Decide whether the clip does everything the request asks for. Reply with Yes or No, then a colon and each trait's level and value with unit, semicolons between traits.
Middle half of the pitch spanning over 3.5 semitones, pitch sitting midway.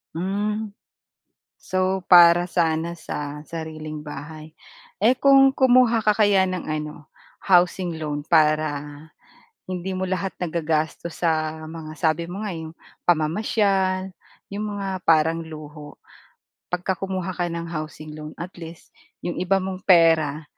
No: average, 3.2 semitones; medium, 170 Hz